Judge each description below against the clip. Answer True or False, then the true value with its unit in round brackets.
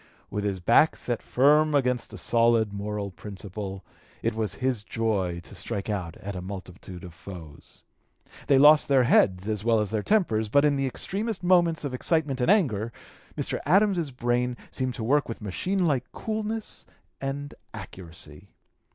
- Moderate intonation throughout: False (6.2 semitones)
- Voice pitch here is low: True (115 Hz)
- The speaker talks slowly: False (165 wpm)